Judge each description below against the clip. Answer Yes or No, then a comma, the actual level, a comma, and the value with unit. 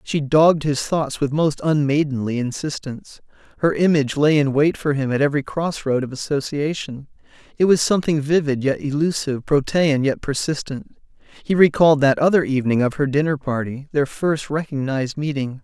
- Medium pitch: Yes, medium, 145 Hz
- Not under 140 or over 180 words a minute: Yes, average, 160 wpm